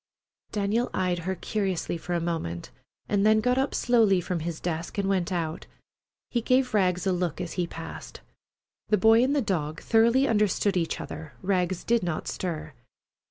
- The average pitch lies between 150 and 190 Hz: Yes, medium, 185 Hz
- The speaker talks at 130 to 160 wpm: No, average, 175 wpm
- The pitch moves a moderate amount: Yes, average, 4.2 semitones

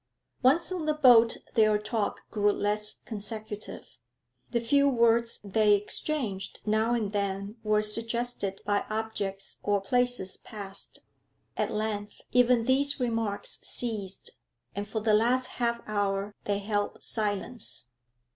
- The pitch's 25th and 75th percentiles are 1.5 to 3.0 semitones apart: Yes, narrow, 2.5 semitones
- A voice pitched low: No, high, 215 Hz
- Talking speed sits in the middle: No, slow, 125 wpm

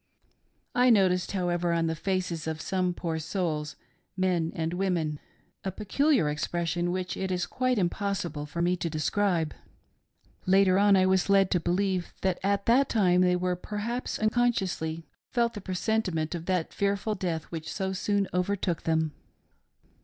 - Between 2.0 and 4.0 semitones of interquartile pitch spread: Yes, average, 2.9 semitones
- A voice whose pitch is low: No, medium, 185 Hz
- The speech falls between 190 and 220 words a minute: No, average, 160 wpm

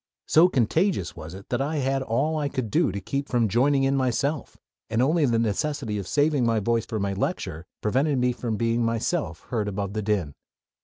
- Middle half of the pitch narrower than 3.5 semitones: No, average, 5.0 semitones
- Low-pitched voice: Yes, low, 120 Hz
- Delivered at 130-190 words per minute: No, fast, 205 wpm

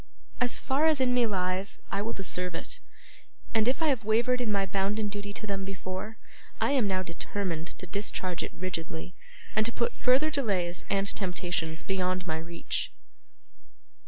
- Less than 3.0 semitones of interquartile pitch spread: No, average, 4.0 semitones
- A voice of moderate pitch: No, high, 200 Hz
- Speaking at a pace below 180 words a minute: Yes, average, 170 wpm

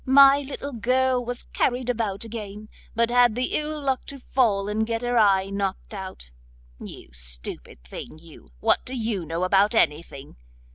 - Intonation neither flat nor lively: Yes, average, 4.4 semitones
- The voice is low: No, high, 220 Hz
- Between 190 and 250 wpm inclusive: No, average, 165 wpm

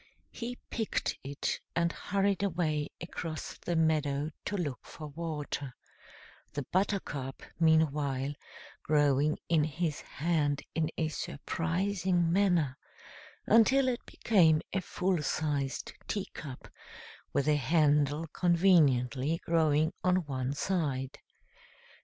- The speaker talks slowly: Yes, slow, 105 wpm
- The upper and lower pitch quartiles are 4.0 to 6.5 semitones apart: No, average, 3.6 semitones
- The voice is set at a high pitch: No, medium, 160 Hz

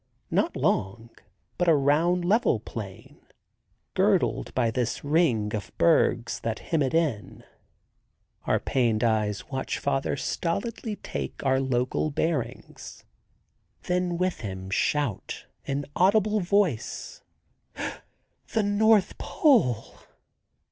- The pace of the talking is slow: Yes, slow, 105 wpm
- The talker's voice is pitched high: No, medium, 140 Hz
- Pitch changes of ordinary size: No, wide, 7.7 semitones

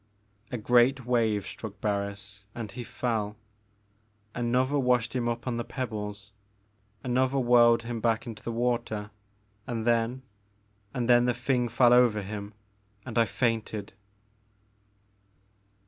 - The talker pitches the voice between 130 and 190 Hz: No, low, 115 Hz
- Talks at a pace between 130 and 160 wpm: Yes, slow, 135 wpm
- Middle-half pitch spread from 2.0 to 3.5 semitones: Yes, average, 2.7 semitones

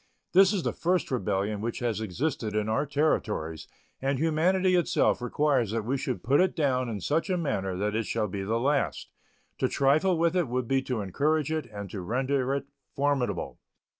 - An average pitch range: No, wide, 6.1 semitones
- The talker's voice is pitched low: Yes, low, 130 Hz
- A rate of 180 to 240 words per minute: Yes, average, 195 wpm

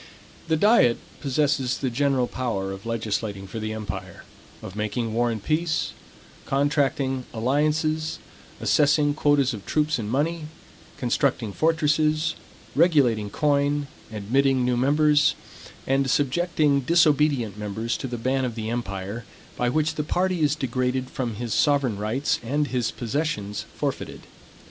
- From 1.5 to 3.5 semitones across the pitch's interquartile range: No, average, 4.5 semitones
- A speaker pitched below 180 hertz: Yes, low, 135 Hz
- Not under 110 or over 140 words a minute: Yes, slow, 135 wpm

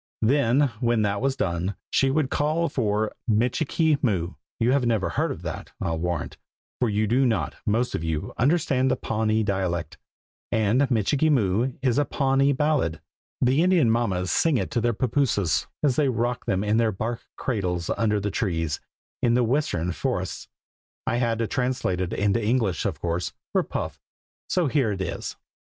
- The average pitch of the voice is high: No, low, 115 Hz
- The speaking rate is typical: Yes, average, 175 wpm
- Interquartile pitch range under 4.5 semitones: No, average, 5.0 semitones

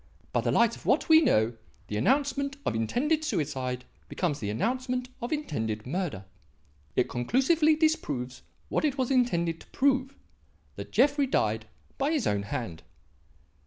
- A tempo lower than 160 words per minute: Yes, average, 150 wpm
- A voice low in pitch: No, high, 240 Hz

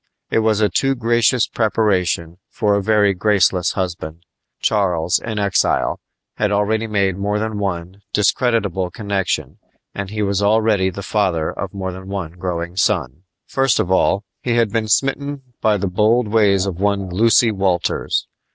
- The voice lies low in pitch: Yes, low, 100 Hz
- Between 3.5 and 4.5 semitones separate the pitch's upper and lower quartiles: No, average, 2.8 semitones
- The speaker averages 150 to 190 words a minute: Yes, average, 160 wpm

